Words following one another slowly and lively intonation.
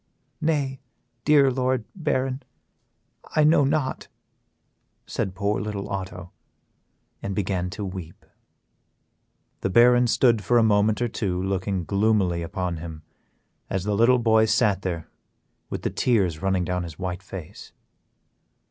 No: slow, 130 wpm; average, 4.8 semitones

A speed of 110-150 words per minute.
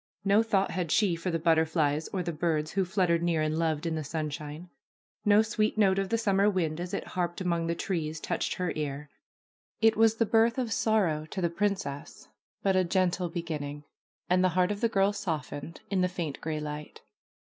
No: average, 200 wpm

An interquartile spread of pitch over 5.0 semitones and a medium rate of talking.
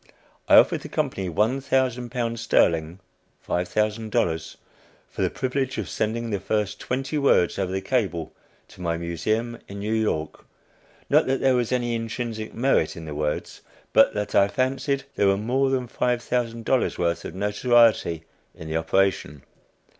Yes: wide, 5.5 semitones; average, 155 wpm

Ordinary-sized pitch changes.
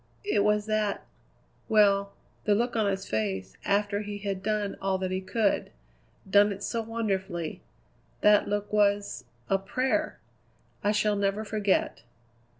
No: narrow, 1.3 semitones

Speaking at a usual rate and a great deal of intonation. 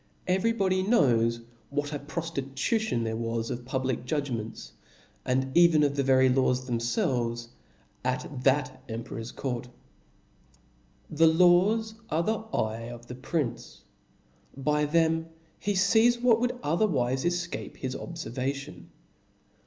No: slow, 130 wpm; wide, 5.7 semitones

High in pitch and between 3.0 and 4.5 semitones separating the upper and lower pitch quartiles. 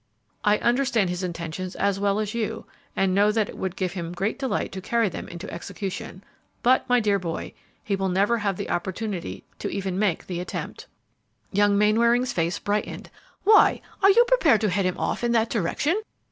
Yes: high, 200 Hz; average, 3.8 semitones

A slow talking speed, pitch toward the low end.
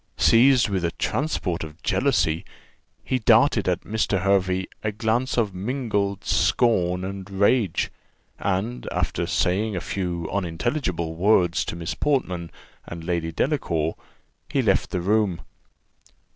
Yes: slow, 130 wpm; very low, 95 Hz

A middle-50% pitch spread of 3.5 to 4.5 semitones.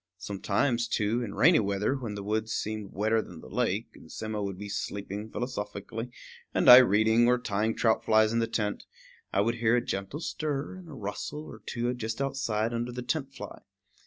No: average, 3.0 semitones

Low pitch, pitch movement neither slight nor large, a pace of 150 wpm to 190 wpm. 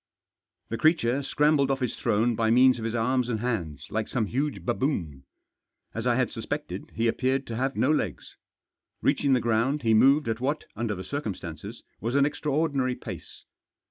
Yes: low, 125 Hz; average, 3.6 semitones; average, 180 wpm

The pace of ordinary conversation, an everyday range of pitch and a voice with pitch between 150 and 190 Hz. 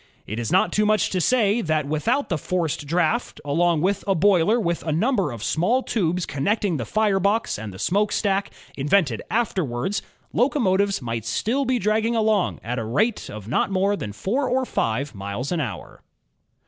No: average, 180 wpm; wide, 7.1 semitones; medium, 185 Hz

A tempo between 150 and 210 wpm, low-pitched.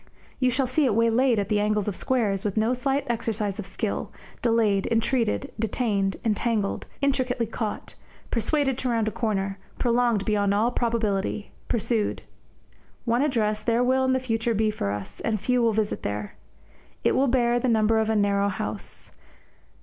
No: average, 170 wpm; high, 225 Hz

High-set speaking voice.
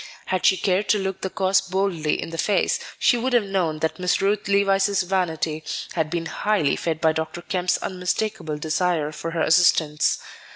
No: medium, 180 Hz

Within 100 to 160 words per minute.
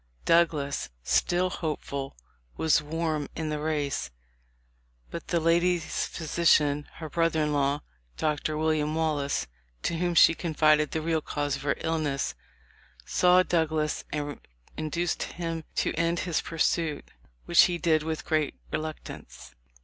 Yes: average, 140 wpm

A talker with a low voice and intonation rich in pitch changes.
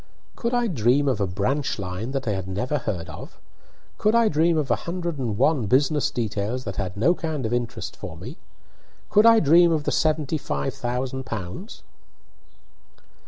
Yes: low, 130 Hz; wide, 7.0 semitones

